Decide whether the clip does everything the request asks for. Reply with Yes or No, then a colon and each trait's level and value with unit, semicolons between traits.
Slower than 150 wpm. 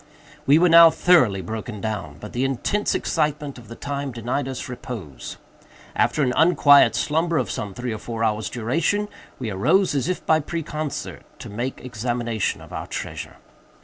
No: average, 170 wpm